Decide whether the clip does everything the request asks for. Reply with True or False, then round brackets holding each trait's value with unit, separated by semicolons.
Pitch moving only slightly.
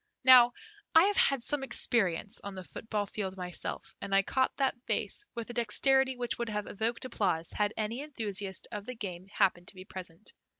False (4.5 semitones)